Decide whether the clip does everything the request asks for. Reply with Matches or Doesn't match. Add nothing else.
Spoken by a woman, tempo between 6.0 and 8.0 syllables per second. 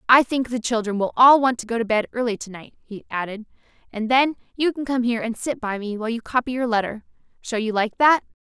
Matches